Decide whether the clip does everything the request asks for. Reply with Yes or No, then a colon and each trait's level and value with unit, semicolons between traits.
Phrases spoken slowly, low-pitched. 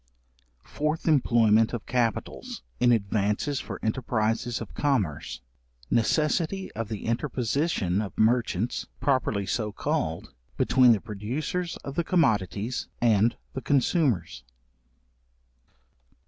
Yes: slow, 105 wpm; low, 115 Hz